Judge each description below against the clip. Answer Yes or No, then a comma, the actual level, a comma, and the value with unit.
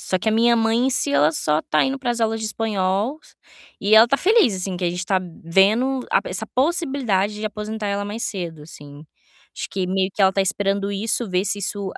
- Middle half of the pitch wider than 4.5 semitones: No, average, 3.4 semitones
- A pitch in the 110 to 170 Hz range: No, high, 205 Hz